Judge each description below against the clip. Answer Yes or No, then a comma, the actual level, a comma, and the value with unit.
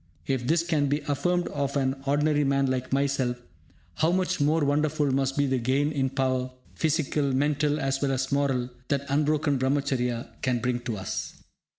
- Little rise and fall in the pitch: Yes, narrow, 2.0 semitones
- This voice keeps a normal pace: Yes, average, 175 wpm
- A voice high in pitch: No, medium, 140 Hz